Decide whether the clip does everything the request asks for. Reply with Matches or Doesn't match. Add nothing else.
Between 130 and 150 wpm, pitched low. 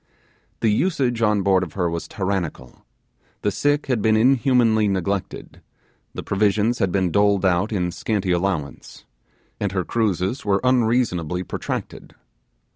Matches